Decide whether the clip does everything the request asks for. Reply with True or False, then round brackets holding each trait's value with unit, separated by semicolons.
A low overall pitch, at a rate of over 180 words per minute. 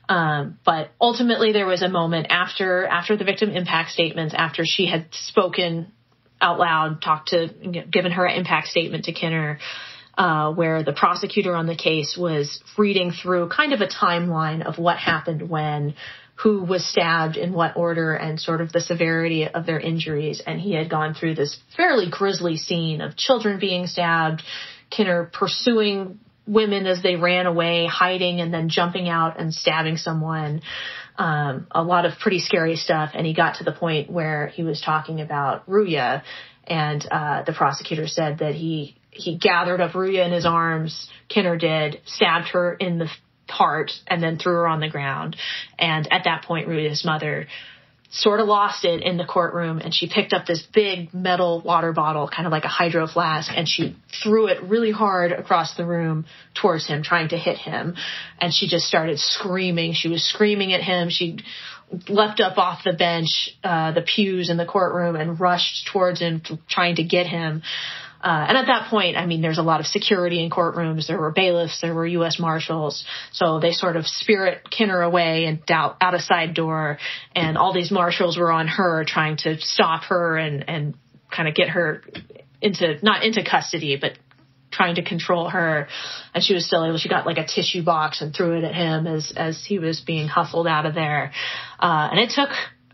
False (170 Hz; 190 wpm)